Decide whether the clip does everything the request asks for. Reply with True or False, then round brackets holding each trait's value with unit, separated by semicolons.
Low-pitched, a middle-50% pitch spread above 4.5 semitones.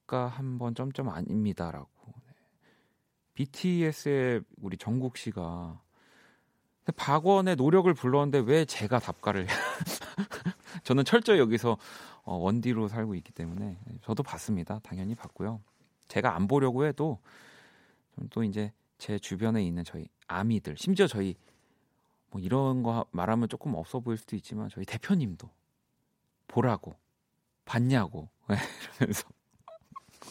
True (115 Hz; 5.6 semitones)